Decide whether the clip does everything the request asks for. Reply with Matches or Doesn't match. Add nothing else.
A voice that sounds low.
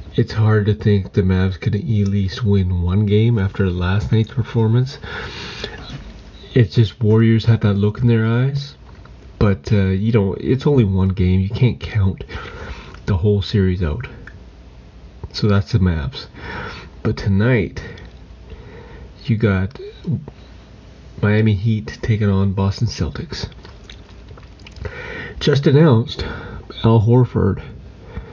Matches